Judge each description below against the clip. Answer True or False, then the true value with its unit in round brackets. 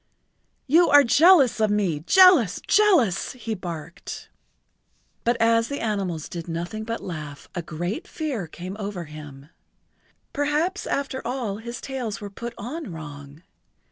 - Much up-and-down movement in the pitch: True (7.7 semitones)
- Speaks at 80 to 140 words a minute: True (135 wpm)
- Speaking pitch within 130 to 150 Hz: False (215 Hz)